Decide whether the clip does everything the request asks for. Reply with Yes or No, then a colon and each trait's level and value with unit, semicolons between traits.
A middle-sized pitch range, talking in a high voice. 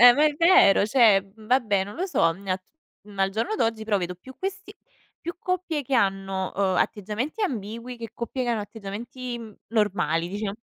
Yes: average, 4.9 semitones; high, 220 Hz